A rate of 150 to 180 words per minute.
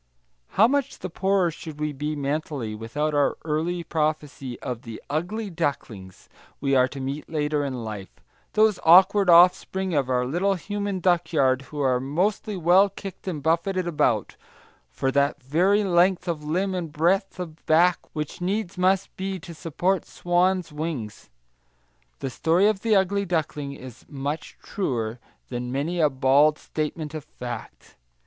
Yes: average, 155 wpm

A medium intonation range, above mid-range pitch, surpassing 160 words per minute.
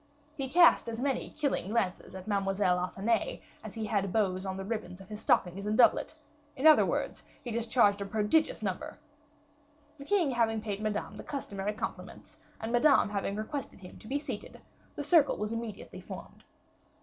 Yes: average, 4.2 semitones; high, 215 Hz; average, 175 wpm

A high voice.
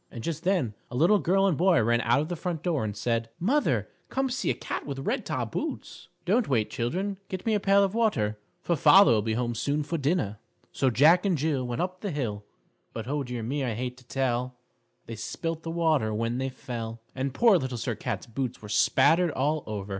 No: low, 135 Hz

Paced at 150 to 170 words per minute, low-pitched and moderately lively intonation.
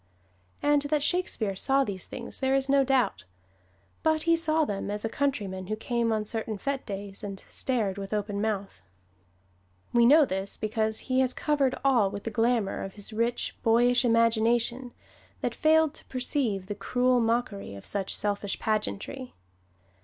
No: average, 165 wpm; high, 230 Hz; average, 4.5 semitones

